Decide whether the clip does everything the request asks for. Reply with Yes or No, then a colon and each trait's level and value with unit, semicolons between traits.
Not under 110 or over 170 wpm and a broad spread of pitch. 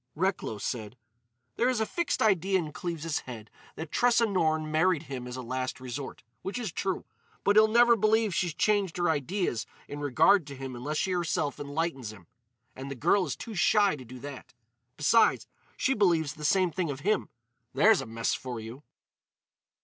No: average, 185 wpm; wide, 6.8 semitones